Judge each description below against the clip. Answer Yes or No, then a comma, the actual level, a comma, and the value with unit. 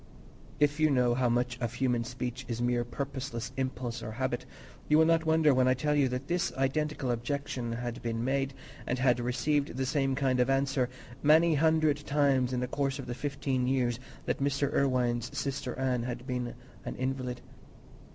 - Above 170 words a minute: Yes, average, 185 wpm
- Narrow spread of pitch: Yes, narrow, 2.3 semitones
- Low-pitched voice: Yes, low, 130 Hz